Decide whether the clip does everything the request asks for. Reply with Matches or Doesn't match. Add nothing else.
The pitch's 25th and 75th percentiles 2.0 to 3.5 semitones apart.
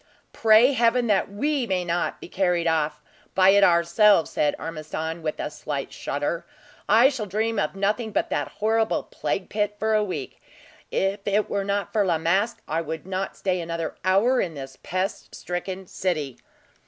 Doesn't match